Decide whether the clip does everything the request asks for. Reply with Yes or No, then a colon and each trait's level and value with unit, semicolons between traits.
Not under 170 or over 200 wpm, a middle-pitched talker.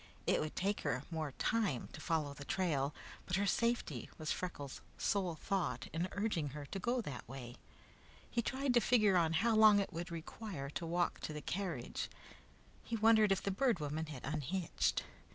Yes: average, 185 wpm; medium, 175 Hz